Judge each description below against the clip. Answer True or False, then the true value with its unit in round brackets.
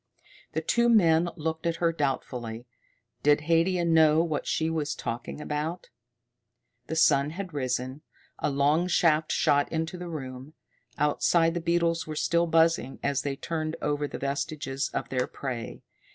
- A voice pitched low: False (155 Hz)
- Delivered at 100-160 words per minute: True (150 wpm)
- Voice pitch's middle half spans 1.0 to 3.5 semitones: True (2.8 semitones)